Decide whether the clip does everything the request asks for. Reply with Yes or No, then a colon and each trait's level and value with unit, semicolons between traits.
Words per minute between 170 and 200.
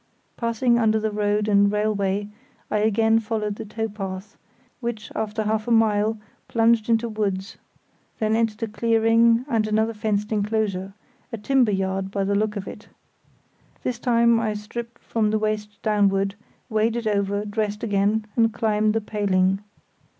No: average, 155 wpm